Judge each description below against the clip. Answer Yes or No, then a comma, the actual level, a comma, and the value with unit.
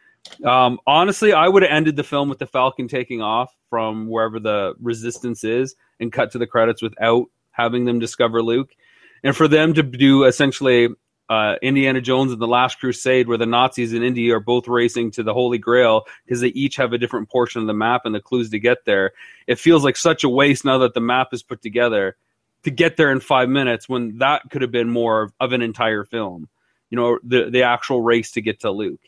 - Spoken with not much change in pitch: Yes, narrow, 2.0 semitones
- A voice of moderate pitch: No, low, 125 Hz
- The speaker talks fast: Yes, fast, 225 wpm